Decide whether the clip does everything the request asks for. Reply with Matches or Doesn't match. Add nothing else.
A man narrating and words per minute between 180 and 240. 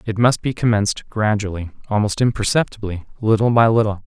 Doesn't match